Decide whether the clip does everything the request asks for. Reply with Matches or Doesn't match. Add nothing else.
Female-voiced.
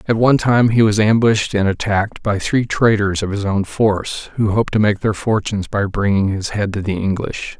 Doesn't match